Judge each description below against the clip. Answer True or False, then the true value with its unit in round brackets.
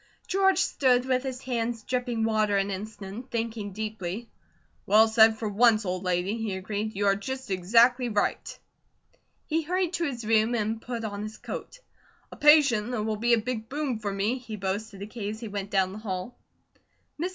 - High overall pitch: True (220 Hz)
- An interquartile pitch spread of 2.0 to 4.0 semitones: True (3.3 semitones)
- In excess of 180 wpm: True (190 wpm)